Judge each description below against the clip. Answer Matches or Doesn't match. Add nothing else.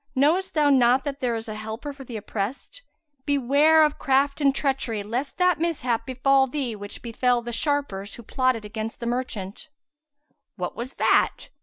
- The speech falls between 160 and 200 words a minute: Matches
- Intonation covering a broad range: Doesn't match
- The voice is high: Matches